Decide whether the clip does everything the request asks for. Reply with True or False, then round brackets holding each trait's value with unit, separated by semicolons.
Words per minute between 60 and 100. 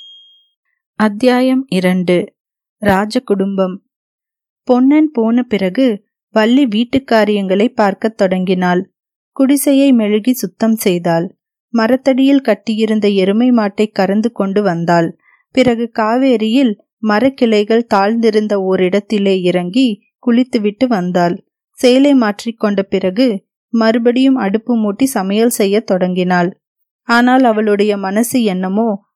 True (85 wpm)